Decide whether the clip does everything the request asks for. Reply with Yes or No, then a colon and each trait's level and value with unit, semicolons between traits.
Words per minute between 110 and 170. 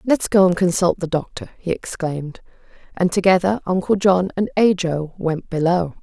Yes: average, 160 wpm